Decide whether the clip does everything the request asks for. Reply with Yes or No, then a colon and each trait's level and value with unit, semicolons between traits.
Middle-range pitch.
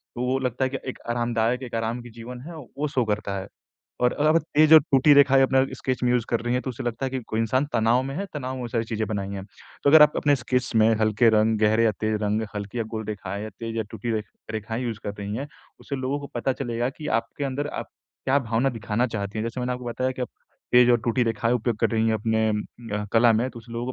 No: low, 120 Hz